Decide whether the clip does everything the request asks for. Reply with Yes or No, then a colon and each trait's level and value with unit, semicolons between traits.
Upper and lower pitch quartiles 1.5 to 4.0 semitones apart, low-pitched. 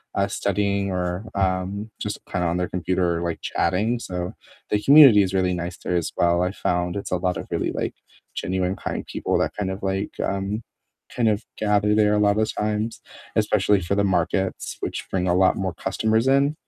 Yes: narrow, 2.5 semitones; very low, 95 Hz